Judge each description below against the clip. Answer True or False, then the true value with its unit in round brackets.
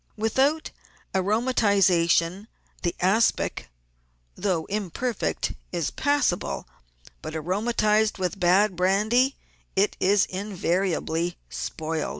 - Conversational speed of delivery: False (90 wpm)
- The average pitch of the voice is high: True (195 Hz)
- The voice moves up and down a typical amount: True (3.7 semitones)